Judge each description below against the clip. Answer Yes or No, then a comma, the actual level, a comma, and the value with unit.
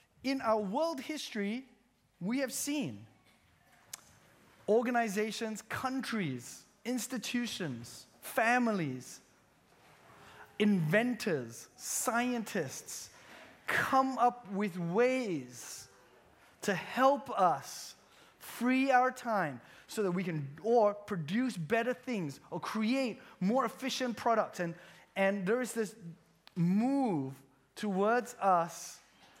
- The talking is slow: Yes, slow, 90 wpm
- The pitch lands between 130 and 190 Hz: No, high, 215 Hz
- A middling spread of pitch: No, wide, 5.7 semitones